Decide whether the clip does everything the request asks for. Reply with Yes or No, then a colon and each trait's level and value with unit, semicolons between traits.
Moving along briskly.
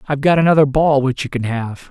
Yes: fast, 250 wpm